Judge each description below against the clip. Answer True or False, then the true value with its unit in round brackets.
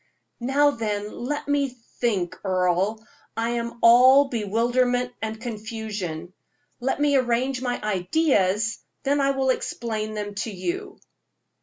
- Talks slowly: True (125 wpm)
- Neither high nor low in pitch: False (235 Hz)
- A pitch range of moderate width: True (3.9 semitones)